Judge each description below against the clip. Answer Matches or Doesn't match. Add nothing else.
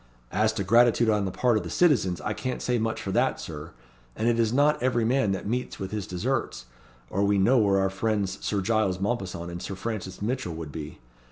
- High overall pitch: Doesn't match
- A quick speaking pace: Matches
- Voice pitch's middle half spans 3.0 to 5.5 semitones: Matches